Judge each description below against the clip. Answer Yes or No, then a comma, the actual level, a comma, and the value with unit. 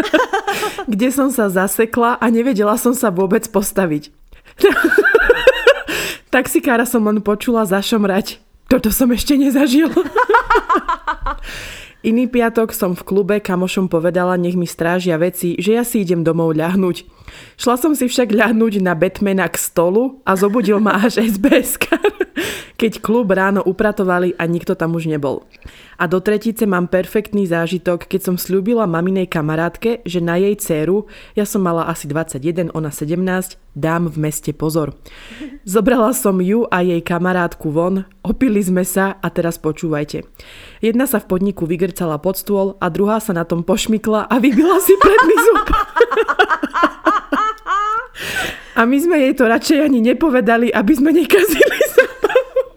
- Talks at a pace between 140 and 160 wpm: Yes, average, 145 wpm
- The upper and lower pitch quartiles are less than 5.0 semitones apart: No, wide, 7.0 semitones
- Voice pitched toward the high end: Yes, high, 215 Hz